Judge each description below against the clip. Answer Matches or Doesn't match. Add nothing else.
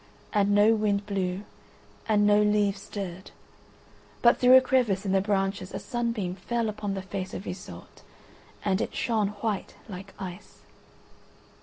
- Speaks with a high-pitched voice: Matches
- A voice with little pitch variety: Matches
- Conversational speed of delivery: Matches